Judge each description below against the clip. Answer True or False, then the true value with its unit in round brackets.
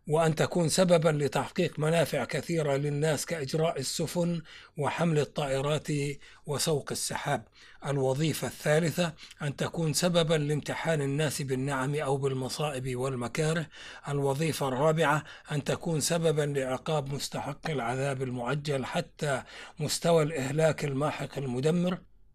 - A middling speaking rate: True (100 wpm)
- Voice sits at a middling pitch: True (150 Hz)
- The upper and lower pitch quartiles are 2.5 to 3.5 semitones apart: True (2.9 semitones)